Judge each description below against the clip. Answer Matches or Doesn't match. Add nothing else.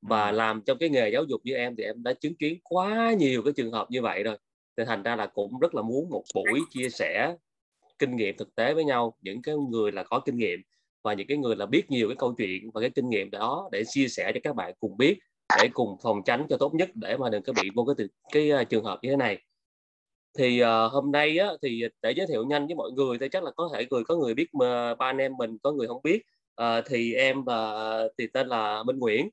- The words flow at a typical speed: Doesn't match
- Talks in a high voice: Doesn't match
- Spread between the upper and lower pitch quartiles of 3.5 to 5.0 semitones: Matches